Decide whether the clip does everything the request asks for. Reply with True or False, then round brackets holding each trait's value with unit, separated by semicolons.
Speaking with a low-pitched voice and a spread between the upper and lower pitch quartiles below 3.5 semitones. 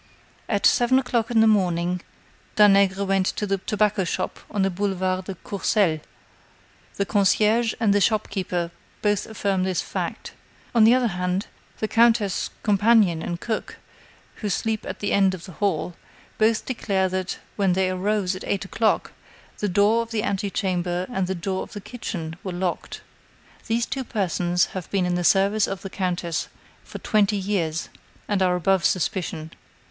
False (195 Hz; 2.6 semitones)